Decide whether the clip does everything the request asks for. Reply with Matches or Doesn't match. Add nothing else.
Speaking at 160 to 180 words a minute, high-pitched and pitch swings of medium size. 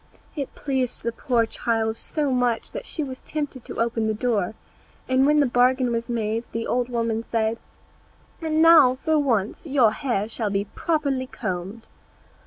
Matches